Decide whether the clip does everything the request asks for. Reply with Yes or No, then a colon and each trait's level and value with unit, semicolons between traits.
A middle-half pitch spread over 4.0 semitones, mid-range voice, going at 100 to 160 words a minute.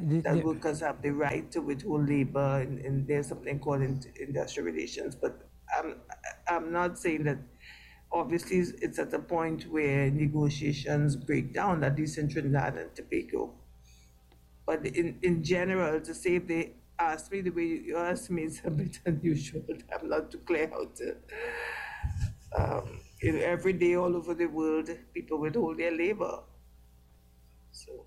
No: average, 3.7 semitones; medium, 155 Hz; average, 155 wpm